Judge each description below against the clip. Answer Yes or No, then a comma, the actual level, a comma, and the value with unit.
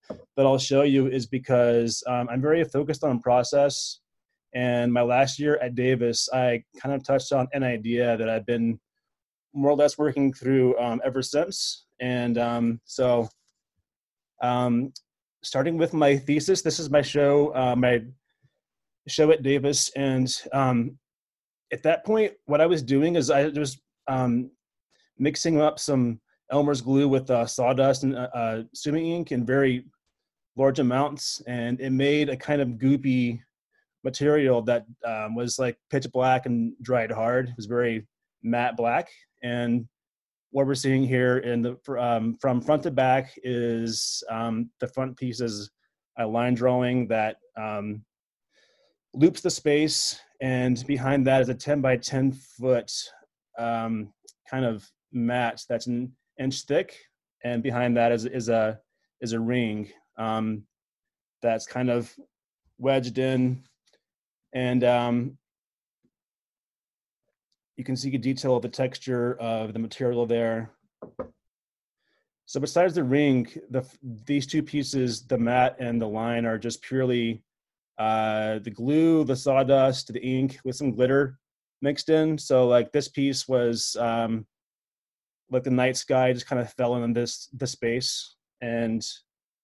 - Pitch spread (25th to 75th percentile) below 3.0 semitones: Yes, narrow, 2.5 semitones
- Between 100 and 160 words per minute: Yes, average, 150 wpm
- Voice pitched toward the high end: No, low, 125 Hz